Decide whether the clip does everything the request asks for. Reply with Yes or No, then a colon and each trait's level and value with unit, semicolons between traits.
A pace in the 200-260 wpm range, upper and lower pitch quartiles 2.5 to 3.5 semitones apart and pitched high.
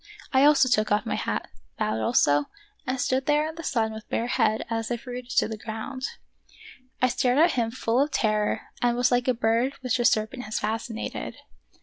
Yes: fast, 205 wpm; average, 3.0 semitones; high, 240 Hz